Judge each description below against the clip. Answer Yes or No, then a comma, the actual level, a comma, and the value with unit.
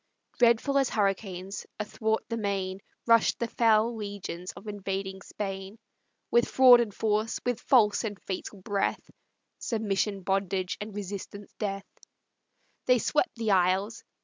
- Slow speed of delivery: Yes, slow, 130 wpm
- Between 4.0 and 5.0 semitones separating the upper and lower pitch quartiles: No, average, 2.7 semitones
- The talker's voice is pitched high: Yes, high, 205 Hz